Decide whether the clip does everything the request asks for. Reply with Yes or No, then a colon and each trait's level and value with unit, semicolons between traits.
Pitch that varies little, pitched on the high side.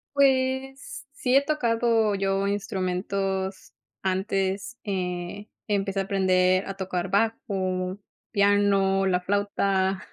Yes: narrow, 2.1 semitones; high, 195 Hz